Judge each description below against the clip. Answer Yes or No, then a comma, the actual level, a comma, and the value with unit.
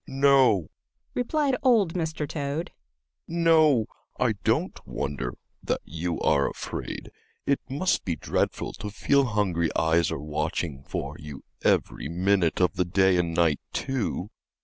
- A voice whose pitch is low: Yes, low, 100 Hz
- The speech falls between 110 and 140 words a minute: Yes, slow, 135 wpm